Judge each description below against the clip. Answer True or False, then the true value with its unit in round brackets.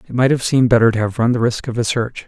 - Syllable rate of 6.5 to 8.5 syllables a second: True (7.0 syllables/s)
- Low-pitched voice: True (120 Hz)